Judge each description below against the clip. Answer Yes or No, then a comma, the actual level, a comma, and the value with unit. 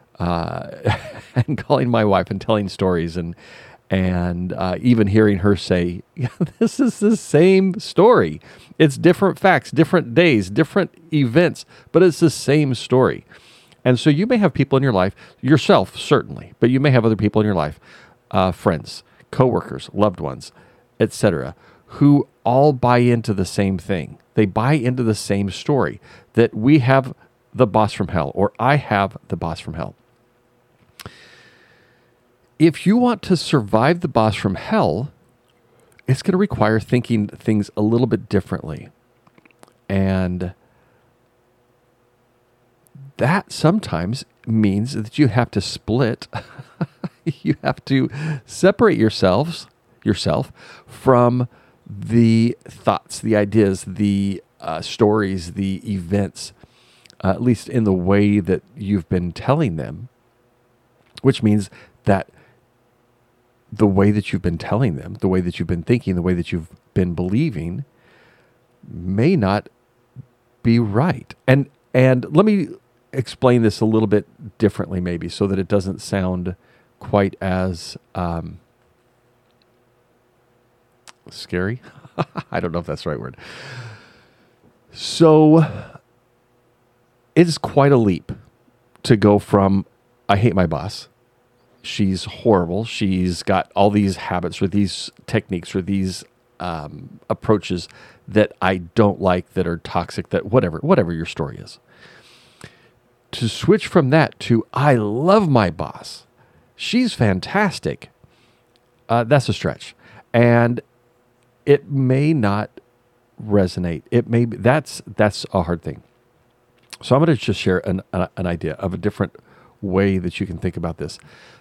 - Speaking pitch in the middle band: No, low, 120 Hz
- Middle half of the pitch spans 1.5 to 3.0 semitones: No, average, 4.3 semitones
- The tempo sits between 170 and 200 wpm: No, average, 140 wpm